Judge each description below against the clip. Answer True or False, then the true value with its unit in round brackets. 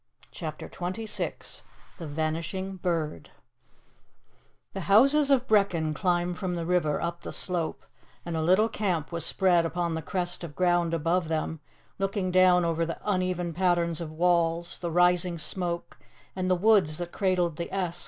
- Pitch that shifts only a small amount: True (1.9 semitones)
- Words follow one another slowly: False (155 wpm)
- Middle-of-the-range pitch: True (175 Hz)